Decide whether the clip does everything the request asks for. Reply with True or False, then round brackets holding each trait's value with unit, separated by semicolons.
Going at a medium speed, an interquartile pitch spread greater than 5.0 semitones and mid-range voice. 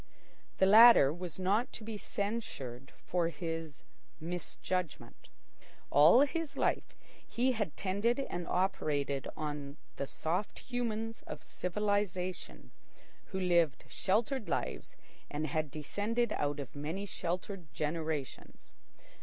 False (110 wpm; 5.5 semitones; 180 Hz)